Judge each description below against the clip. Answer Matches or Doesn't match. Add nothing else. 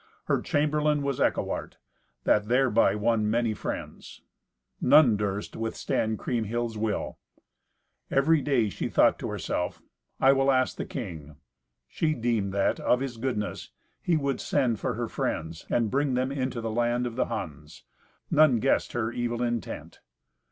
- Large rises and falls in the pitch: Doesn't match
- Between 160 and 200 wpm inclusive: Doesn't match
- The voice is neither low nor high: Doesn't match